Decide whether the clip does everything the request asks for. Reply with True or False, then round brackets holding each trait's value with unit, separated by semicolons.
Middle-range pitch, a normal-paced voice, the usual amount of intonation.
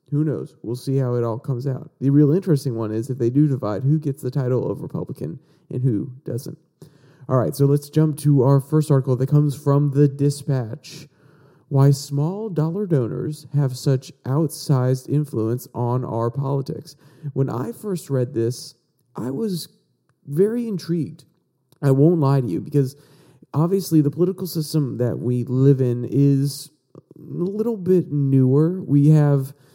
True (145 Hz; 165 wpm; 3.0 semitones)